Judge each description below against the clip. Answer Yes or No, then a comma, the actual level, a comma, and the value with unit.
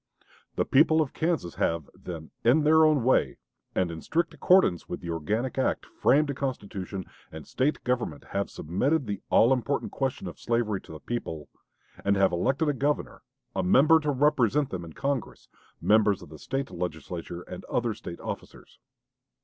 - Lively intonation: Yes, wide, 8.1 semitones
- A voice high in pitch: No, low, 120 Hz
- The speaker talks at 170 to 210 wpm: Yes, average, 175 wpm